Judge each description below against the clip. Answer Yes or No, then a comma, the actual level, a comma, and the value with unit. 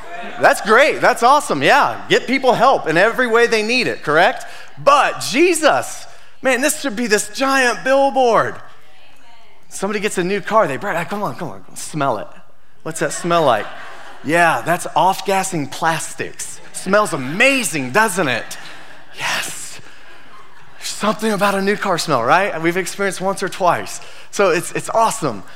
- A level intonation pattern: No, average, 4.2 semitones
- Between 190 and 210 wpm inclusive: No, average, 160 wpm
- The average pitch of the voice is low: No, high, 210 Hz